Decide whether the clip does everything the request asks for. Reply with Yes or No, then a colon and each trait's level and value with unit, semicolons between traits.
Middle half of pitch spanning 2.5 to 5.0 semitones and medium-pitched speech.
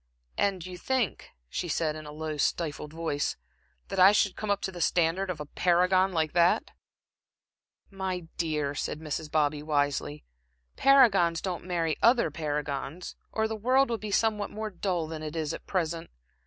Yes: average, 4.1 semitones; medium, 170 Hz